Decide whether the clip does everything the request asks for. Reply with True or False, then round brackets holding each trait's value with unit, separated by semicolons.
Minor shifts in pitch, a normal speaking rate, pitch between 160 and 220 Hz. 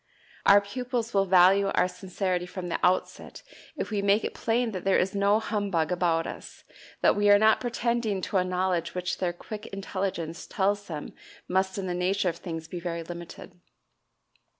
True (2.3 semitones; 180 wpm; 190 Hz)